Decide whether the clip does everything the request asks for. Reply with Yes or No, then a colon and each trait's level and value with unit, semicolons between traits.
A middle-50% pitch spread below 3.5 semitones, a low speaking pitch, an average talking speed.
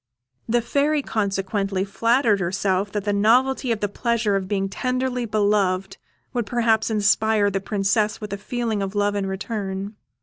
No: average, 2.8 semitones; high, 210 Hz; average, 160 wpm